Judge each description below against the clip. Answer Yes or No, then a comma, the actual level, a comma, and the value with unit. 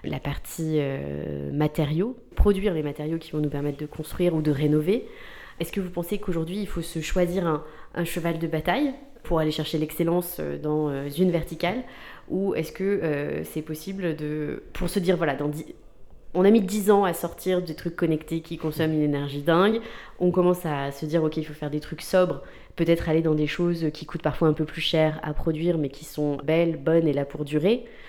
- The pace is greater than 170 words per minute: Yes, average, 215 wpm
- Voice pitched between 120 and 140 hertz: No, medium, 160 Hz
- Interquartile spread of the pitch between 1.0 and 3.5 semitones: Yes, average, 2.7 semitones